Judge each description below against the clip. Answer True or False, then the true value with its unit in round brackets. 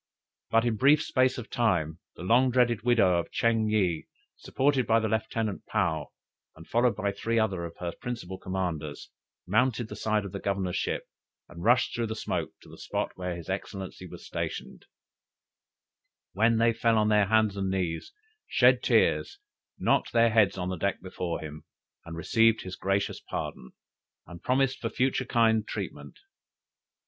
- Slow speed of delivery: False (170 wpm)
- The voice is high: False (110 Hz)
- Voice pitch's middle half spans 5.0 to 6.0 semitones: False (3.9 semitones)